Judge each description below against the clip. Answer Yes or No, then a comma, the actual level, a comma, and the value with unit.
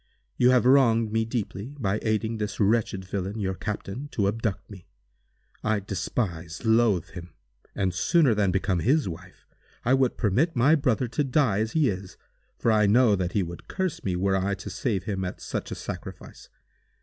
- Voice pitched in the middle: No, low, 105 Hz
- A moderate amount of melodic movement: Yes, average, 4.2 semitones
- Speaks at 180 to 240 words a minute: Yes, average, 185 wpm